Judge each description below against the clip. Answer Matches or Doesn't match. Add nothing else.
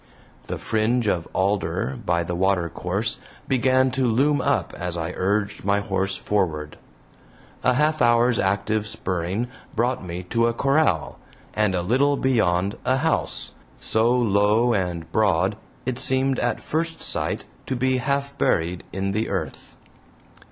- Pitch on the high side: Doesn't match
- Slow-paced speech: Doesn't match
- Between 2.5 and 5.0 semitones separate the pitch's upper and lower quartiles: Doesn't match